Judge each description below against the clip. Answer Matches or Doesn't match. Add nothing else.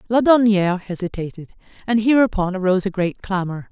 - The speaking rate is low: Matches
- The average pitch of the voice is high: Matches